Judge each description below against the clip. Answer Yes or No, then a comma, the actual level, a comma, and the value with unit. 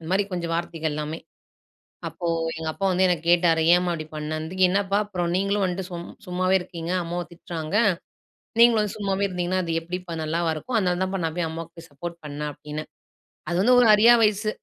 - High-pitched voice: No, medium, 175 Hz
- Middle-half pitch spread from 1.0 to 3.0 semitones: Yes, narrow, 2.5 semitones